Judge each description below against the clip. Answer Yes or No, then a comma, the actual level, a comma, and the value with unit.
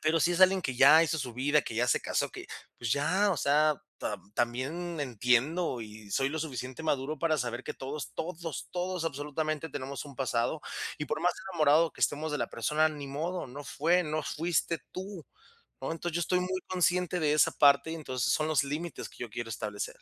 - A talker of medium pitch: Yes, medium, 150 Hz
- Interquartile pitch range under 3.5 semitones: No, average, 3.8 semitones